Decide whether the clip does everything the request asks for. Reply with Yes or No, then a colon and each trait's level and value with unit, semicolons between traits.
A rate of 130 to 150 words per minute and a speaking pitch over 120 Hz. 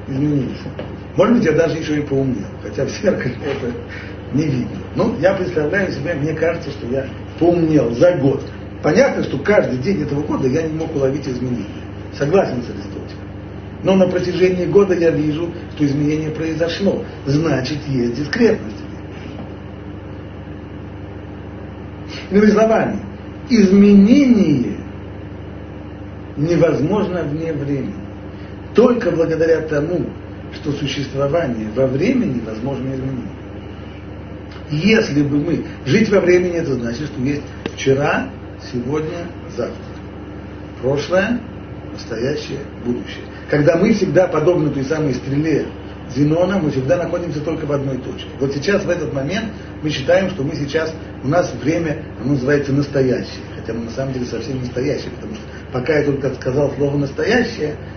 Yes: average, 135 wpm; low, 135 Hz